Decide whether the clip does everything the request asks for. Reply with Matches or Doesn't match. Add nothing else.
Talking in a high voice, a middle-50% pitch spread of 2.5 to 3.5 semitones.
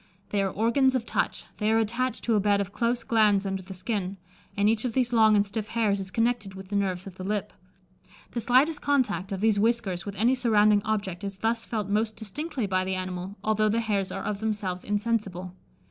Matches